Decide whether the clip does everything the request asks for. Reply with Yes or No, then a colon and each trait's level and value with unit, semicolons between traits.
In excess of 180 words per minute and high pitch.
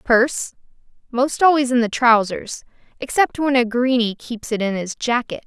No: average, 155 wpm; high, 245 Hz